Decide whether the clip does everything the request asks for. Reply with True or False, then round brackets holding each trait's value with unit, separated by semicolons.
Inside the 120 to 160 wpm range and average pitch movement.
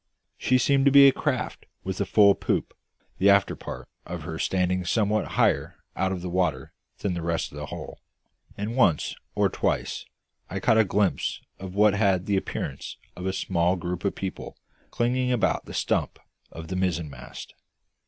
False (180 wpm; 3.1 semitones)